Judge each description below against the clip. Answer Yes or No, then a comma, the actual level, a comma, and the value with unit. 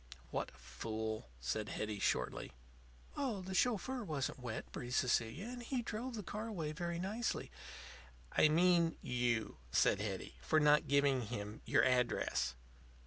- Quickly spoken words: No, average, 145 wpm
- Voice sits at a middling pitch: Yes, medium, 150 Hz